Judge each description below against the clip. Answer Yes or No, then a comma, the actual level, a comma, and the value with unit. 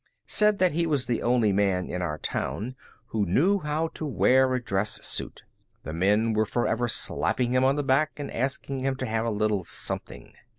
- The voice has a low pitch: Yes, low, 125 Hz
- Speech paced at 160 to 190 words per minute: No, average, 200 wpm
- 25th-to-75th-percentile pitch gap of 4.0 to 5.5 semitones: Yes, average, 4.8 semitones